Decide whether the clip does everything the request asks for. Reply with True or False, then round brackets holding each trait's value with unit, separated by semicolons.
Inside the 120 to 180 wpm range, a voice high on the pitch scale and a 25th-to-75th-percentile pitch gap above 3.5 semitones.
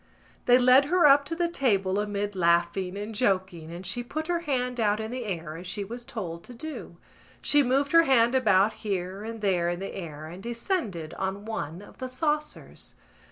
False (200 wpm; 215 Hz; 5.5 semitones)